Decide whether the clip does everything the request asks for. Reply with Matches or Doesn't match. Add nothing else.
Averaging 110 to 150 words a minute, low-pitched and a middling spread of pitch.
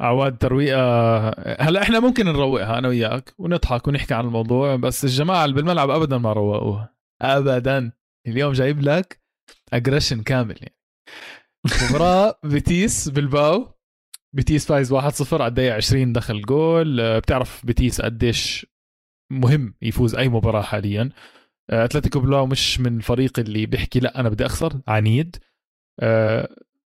Matches